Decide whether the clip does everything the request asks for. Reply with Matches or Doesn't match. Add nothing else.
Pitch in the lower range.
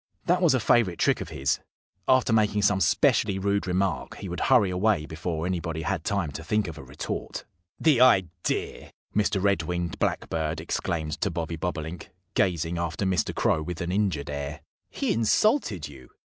Matches